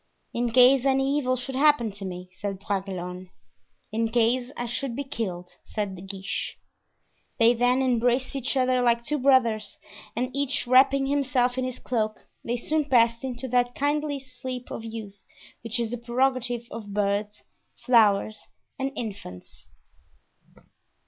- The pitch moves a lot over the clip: No, average, 3.2 semitones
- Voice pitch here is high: Yes, high, 240 Hz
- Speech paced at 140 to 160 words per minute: Yes, average, 150 wpm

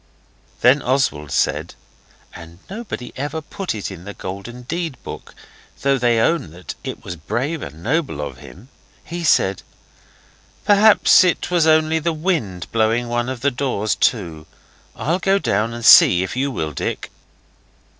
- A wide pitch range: Yes, wide, 8.5 semitones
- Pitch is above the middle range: No, low, 125 Hz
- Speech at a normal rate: Yes, average, 155 wpm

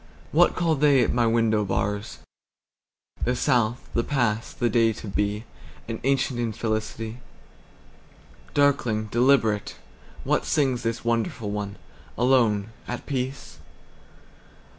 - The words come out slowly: Yes, slow, 95 wpm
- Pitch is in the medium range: No, low, 115 Hz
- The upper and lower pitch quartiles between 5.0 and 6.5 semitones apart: No, average, 2.8 semitones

